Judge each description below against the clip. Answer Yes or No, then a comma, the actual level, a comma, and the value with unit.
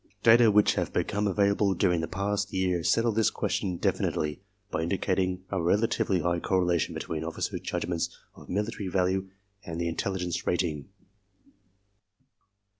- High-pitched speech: No, very low, 95 Hz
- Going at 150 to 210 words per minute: No, average, 140 wpm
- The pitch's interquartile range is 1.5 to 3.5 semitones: Yes, average, 2.7 semitones